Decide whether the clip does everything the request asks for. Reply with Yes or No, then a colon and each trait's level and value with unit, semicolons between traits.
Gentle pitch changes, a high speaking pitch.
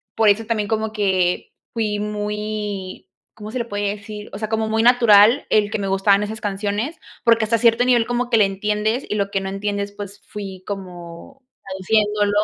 Yes: narrow, 1.7 semitones; high, 210 Hz